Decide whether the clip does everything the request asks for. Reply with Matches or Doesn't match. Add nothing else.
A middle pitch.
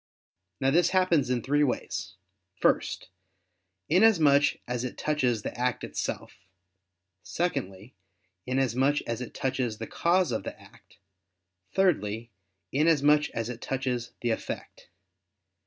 Doesn't match